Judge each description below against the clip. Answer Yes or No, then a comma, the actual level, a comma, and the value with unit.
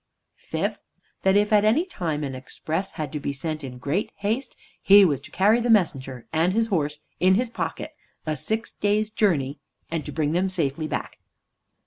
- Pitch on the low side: No, medium, 175 Hz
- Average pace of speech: Yes, average, 185 wpm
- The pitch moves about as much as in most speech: No, wide, 5.8 semitones